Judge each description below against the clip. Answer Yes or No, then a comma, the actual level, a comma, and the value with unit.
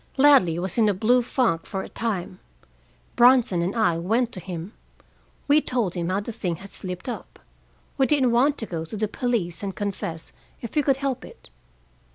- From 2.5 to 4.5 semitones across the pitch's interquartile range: No, wide, 5.4 semitones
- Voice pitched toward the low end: No, high, 210 Hz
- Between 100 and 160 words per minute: No, average, 195 wpm